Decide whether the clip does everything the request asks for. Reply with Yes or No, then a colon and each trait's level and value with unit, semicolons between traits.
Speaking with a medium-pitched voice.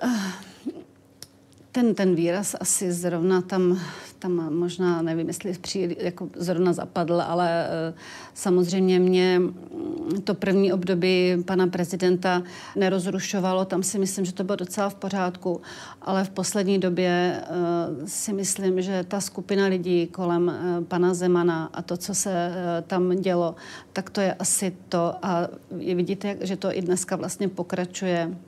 Yes: medium, 180 Hz